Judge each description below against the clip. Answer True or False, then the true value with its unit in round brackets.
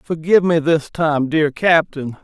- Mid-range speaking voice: True (155 Hz)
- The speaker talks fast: False (160 wpm)